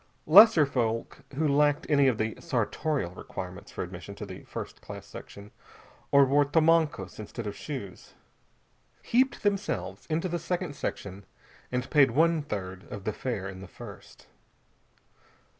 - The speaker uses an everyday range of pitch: No, wide, 7.6 semitones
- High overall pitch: No, medium, 140 Hz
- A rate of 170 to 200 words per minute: No, average, 145 wpm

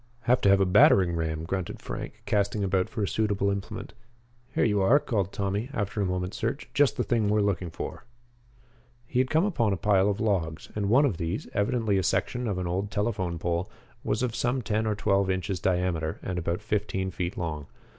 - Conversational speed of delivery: No, fast, 210 wpm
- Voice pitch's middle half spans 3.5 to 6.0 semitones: No, average, 3.0 semitones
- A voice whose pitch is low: Yes, low, 100 Hz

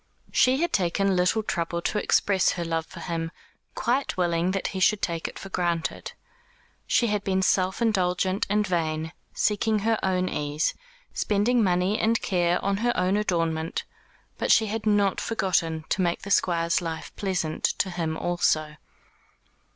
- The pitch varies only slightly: No, average, 3.5 semitones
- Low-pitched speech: No, medium, 185 Hz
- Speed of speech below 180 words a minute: Yes, average, 160 wpm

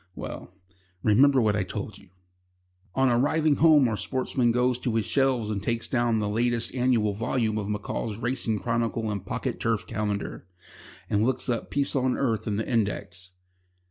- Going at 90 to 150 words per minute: No, average, 170 wpm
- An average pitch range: Yes, average, 3.3 semitones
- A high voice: No, low, 115 Hz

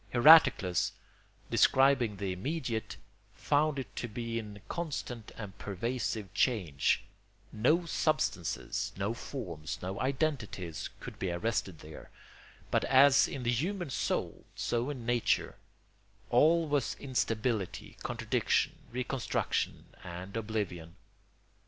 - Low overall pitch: Yes, low, 115 Hz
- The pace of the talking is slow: Yes, slow, 110 wpm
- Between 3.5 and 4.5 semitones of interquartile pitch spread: No, wide, 5.6 semitones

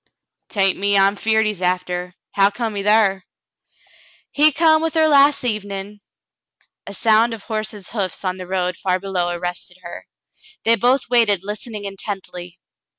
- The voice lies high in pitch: Yes, high, 200 Hz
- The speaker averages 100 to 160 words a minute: No, average, 175 wpm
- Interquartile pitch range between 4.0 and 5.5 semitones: No, average, 3.3 semitones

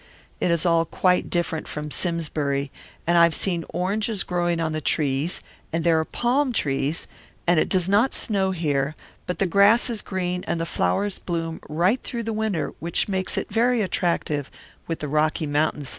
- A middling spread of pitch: Yes, average, 3.8 semitones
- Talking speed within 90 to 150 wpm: No, average, 185 wpm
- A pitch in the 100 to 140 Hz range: No, medium, 170 Hz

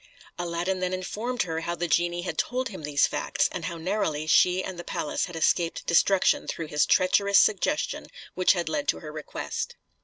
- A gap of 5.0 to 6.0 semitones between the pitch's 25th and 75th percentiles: No, narrow, 2.6 semitones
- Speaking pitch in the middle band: Yes, medium, 175 Hz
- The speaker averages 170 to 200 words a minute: Yes, average, 190 wpm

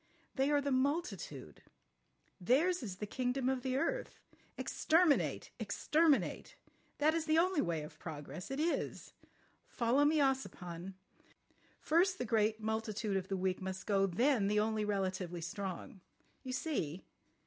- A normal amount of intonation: No, wide, 7.2 semitones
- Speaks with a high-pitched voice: Yes, high, 230 Hz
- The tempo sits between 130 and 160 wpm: Yes, average, 140 wpm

